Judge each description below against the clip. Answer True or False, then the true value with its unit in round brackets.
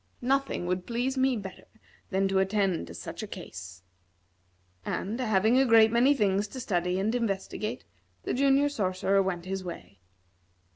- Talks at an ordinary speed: True (155 wpm)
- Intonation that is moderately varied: True (4.7 semitones)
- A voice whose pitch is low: False (200 Hz)